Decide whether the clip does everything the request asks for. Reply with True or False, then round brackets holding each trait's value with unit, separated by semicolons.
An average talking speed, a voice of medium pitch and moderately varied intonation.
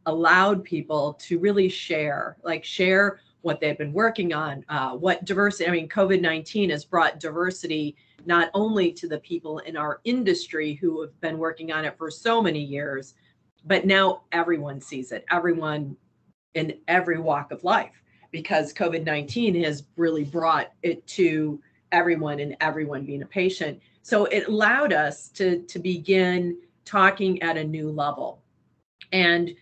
True (155 wpm; 165 Hz; 3.3 semitones)